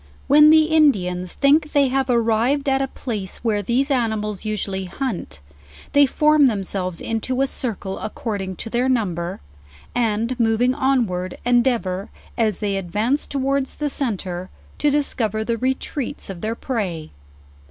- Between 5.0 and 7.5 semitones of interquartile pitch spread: Yes, average, 5.3 semitones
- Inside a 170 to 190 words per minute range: No, average, 150 wpm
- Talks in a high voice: Yes, high, 230 Hz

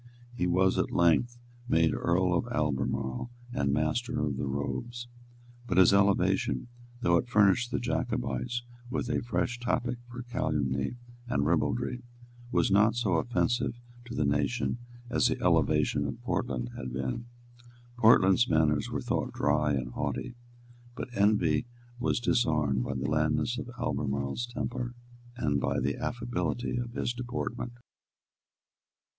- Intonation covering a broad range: Yes, wide, 8.4 semitones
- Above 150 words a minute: No, average, 140 wpm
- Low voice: Yes, very low, 95 Hz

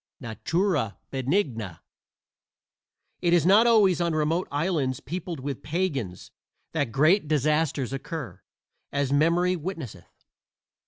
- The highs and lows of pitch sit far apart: No, average, 4.8 semitones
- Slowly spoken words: Yes, slow, 105 wpm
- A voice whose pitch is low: No, medium, 155 Hz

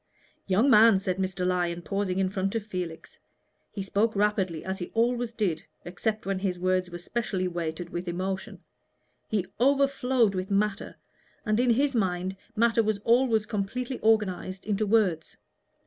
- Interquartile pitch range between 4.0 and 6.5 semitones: No, average, 3.4 semitones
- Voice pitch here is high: Yes, high, 195 Hz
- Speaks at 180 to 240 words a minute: No, average, 155 wpm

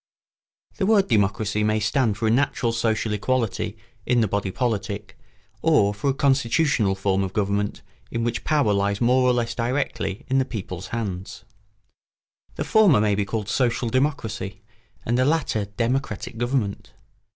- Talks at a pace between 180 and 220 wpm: No, average, 160 wpm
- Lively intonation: No, average, 4.0 semitones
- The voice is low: Yes, low, 115 Hz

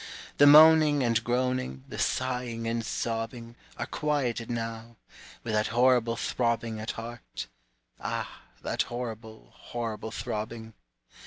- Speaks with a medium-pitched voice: No, low, 115 Hz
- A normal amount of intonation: No, narrow, 1.9 semitones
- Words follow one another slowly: Yes, slow, 115 wpm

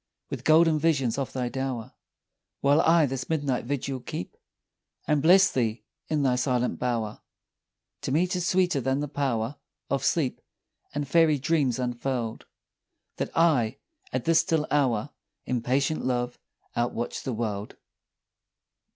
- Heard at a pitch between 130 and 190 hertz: Yes, low, 135 Hz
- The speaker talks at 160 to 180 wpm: No, average, 140 wpm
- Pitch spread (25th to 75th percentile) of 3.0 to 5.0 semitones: Yes, average, 3.8 semitones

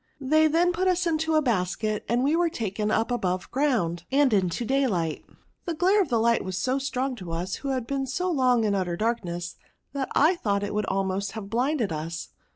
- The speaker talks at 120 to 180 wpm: No, fast, 205 wpm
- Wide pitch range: Yes, wide, 6.7 semitones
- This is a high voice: Yes, high, 235 Hz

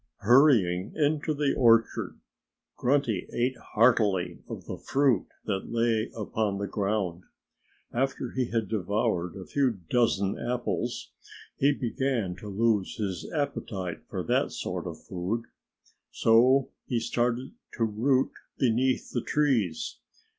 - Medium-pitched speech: No, low, 115 Hz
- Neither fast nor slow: No, slow, 125 wpm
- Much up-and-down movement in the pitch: No, average, 4.4 semitones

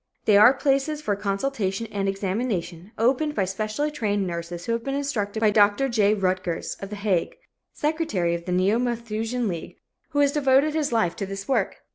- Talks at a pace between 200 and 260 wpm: No, average, 185 wpm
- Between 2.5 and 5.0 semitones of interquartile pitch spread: No, wide, 5.5 semitones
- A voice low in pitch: No, high, 215 Hz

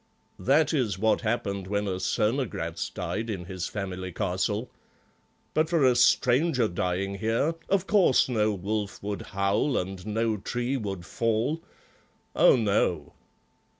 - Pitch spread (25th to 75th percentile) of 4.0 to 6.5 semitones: Yes, average, 4.3 semitones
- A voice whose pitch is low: Yes, low, 110 Hz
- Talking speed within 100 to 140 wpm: Yes, slow, 135 wpm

